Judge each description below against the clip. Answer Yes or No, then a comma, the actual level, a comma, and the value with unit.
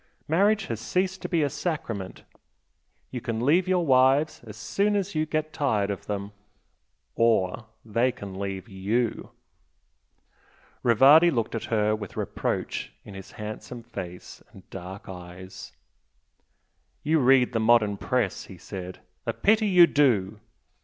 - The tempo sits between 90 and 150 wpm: Yes, average, 140 wpm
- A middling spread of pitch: No, wide, 7.2 semitones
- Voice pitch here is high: No, low, 115 Hz